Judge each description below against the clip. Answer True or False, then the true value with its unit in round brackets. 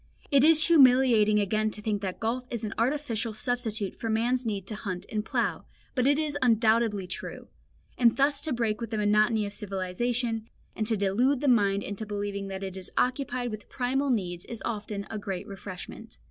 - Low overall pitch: False (220 Hz)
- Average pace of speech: True (190 wpm)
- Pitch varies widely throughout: False (3.3 semitones)